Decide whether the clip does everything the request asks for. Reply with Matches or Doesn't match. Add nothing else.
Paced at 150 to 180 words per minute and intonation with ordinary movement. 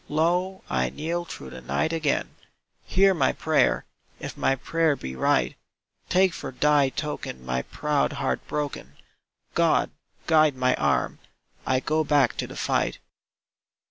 Doesn't match